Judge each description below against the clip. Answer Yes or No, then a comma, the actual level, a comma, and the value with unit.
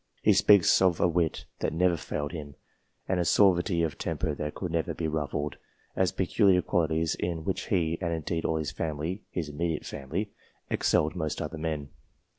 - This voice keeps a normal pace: Yes, average, 180 wpm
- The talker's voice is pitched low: Yes, very low, 80 Hz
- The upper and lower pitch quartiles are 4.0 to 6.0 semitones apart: No, narrow, 2.4 semitones